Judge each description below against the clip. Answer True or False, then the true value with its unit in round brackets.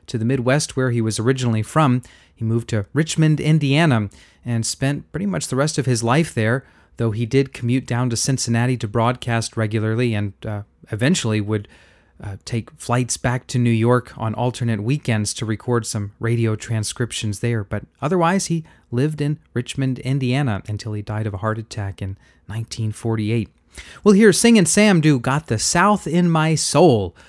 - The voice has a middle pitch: False (120 Hz)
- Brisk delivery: False (180 wpm)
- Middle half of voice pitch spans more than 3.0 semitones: True (4.1 semitones)